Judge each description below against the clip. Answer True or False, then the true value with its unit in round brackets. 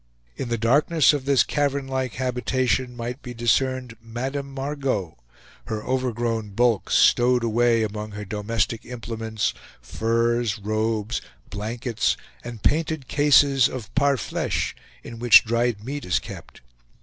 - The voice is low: True (120 Hz)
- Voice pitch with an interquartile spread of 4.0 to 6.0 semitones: False (2.8 semitones)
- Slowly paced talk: True (130 wpm)